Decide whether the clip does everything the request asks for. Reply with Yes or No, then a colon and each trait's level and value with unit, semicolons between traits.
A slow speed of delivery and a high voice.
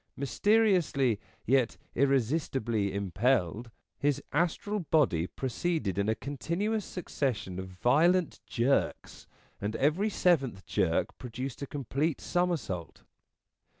No: slow, 115 wpm; low, 135 Hz